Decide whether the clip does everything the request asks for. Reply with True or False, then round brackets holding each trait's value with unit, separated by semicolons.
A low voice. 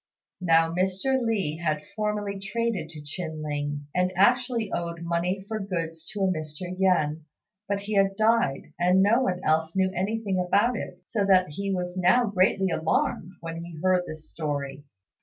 False (185 Hz)